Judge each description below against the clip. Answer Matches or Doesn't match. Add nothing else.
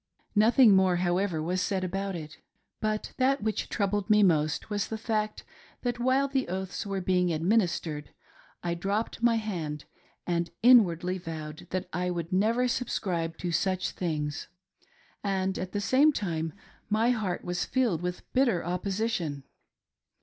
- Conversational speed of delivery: Matches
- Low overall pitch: Doesn't match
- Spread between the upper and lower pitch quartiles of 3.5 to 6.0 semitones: Matches